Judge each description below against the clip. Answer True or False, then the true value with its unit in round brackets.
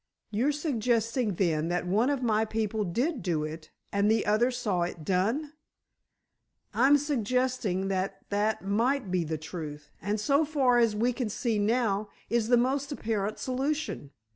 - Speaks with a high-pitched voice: True (220 Hz)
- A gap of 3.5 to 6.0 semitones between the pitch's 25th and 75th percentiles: True (4.8 semitones)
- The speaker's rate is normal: True (160 wpm)